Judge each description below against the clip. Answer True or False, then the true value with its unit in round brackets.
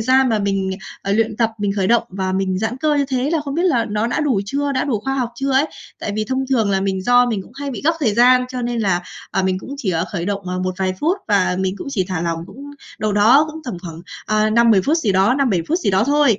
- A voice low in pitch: False (220 Hz)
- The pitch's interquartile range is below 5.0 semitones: False (5.6 semitones)